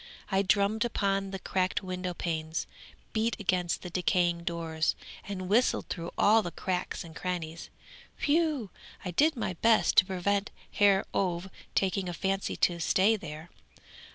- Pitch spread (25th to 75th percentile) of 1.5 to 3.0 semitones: Yes, average, 2.7 semitones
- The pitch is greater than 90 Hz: Yes, medium, 185 Hz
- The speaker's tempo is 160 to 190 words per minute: No, average, 150 wpm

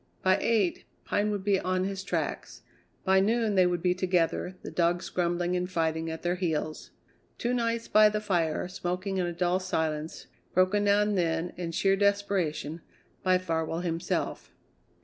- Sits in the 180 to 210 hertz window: Yes, medium, 185 Hz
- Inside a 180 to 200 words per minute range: No, average, 170 wpm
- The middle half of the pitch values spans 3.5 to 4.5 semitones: No, average, 2.7 semitones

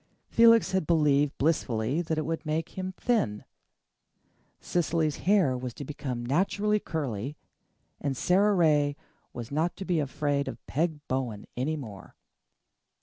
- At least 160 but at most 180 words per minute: No, average, 140 wpm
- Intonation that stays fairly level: No, average, 4.6 semitones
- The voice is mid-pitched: Yes, medium, 150 Hz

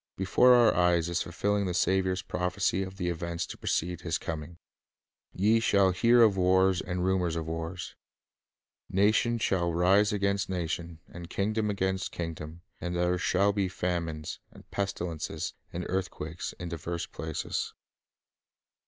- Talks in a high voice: No, very low, 90 Hz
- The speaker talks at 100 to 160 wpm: Yes, average, 145 wpm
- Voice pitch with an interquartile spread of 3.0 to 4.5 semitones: No, narrow, 2.4 semitones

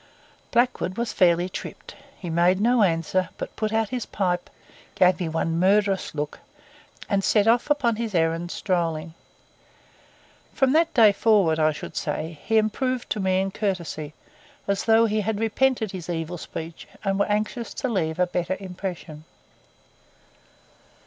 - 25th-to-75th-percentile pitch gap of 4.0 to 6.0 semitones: Yes, average, 4.5 semitones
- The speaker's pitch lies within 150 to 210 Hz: Yes, high, 190 Hz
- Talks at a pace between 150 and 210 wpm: Yes, average, 155 wpm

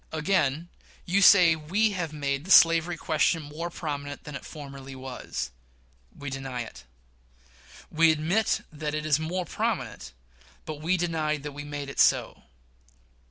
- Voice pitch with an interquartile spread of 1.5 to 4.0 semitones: Yes, average, 2.8 semitones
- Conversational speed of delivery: Yes, average, 150 wpm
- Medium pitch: Yes, medium, 155 Hz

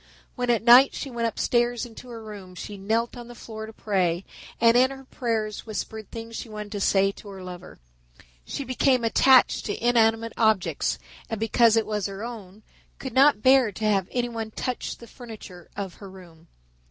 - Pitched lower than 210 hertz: No, high, 225 Hz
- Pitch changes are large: No, average, 2.8 semitones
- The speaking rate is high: No, average, 190 wpm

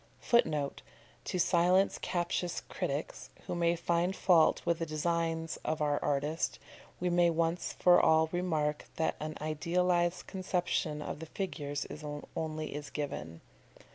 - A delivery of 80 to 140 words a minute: Yes, slow, 135 wpm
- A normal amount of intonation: No, narrow, 2.3 semitones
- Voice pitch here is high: No, medium, 165 Hz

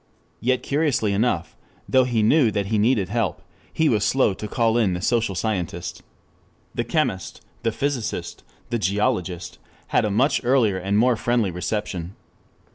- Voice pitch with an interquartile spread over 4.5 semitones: No, average, 3.9 semitones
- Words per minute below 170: Yes, average, 160 wpm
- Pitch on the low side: Yes, low, 110 Hz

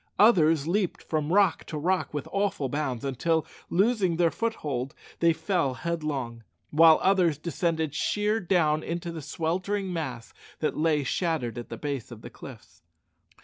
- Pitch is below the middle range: No, medium, 160 Hz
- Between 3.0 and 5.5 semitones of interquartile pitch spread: Yes, average, 3.8 semitones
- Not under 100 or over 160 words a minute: Yes, average, 150 wpm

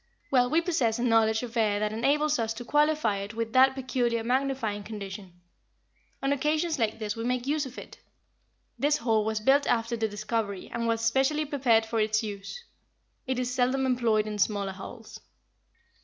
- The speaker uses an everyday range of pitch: Yes, average, 3.5 semitones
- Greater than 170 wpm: Yes, average, 180 wpm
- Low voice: No, high, 230 Hz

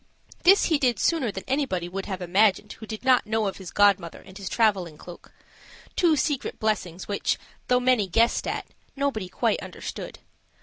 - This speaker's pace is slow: No, average, 175 wpm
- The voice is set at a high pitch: Yes, high, 215 Hz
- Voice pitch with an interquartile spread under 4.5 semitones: No, average, 5.1 semitones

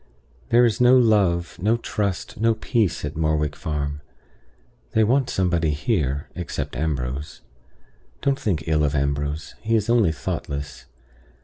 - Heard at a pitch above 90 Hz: No, very low, 85 Hz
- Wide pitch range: Yes, wide, 7.0 semitones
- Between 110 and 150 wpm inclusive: Yes, slow, 135 wpm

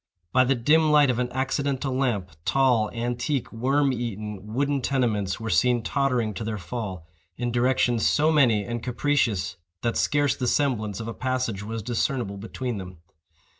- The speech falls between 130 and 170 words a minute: Yes, average, 165 wpm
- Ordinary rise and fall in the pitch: Yes, average, 3.6 semitones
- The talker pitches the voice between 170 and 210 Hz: No, low, 120 Hz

